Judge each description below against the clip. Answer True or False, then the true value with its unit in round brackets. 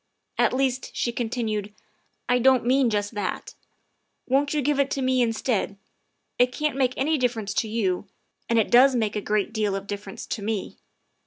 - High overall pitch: True (235 Hz)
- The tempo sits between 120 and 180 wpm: False (190 wpm)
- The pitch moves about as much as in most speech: True (3.8 semitones)